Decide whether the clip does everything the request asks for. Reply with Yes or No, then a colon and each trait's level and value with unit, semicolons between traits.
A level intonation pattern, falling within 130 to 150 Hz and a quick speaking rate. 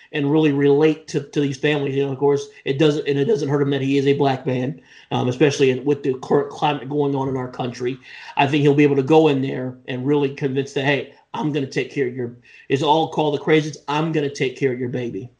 Yes: narrow, 1.9 semitones; medium, 140 Hz; fast, 275 wpm